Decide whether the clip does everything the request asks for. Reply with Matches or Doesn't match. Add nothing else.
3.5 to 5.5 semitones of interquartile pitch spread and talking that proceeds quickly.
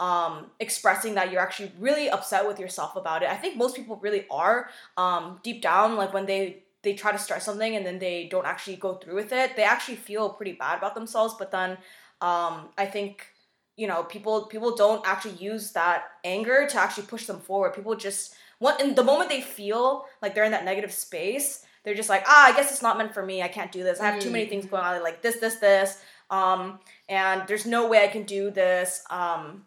Doesn't match